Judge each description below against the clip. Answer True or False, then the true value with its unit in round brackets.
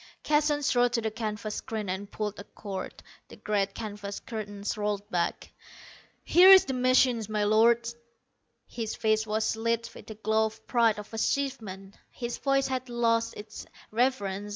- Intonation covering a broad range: False (2.5 semitones)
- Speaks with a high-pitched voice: True (220 Hz)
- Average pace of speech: True (160 wpm)